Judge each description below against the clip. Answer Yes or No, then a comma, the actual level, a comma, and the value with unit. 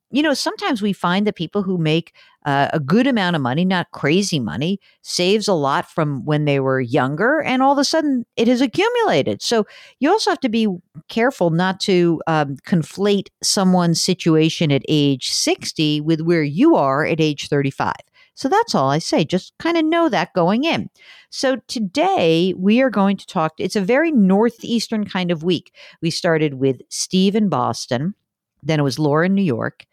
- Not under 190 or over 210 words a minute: Yes, average, 195 wpm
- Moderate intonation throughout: No, wide, 6.6 semitones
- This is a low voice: No, medium, 185 Hz